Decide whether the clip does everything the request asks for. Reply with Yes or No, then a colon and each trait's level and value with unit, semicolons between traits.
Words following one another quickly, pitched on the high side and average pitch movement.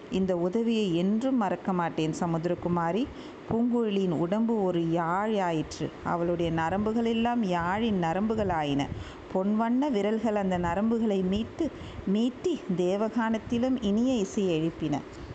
No: average, 95 wpm; high, 200 Hz; average, 4.7 semitones